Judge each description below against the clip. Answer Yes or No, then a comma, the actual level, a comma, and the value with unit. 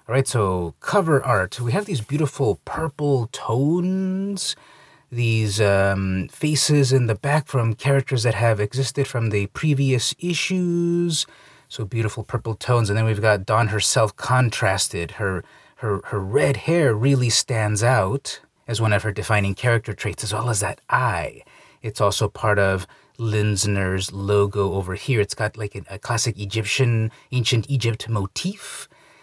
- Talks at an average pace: Yes, average, 150 wpm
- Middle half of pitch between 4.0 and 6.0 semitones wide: Yes, average, 4.7 semitones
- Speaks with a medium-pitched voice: No, low, 115 Hz